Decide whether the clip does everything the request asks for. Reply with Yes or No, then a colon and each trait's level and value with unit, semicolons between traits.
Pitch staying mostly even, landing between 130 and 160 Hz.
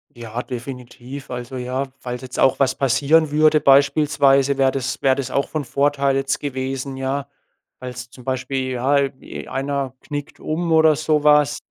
Yes: narrow, 1.7 semitones; low, 135 Hz